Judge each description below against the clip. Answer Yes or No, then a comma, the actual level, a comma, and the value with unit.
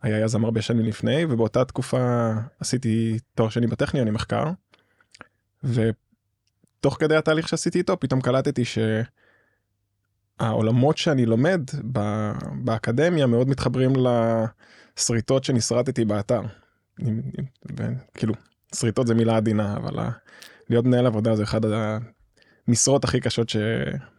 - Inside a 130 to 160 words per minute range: No, average, 105 wpm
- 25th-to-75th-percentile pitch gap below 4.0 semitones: Yes, average, 2.9 semitones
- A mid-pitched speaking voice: No, low, 120 Hz